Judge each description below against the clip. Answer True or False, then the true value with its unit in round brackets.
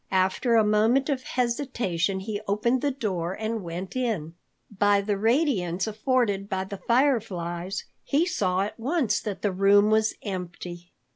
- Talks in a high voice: True (210 Hz)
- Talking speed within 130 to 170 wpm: True (150 wpm)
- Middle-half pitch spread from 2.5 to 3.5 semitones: False (4.0 semitones)